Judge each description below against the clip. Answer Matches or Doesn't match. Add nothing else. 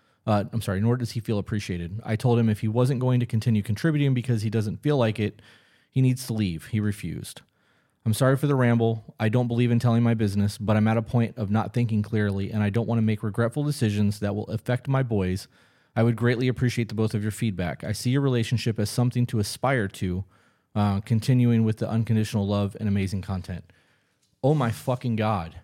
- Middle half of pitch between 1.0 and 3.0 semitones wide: Matches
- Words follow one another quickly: Matches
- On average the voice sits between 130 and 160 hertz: Doesn't match